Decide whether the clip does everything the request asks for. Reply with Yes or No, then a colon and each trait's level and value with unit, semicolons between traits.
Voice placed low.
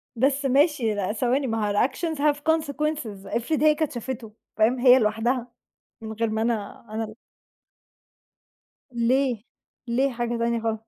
No: high, 240 Hz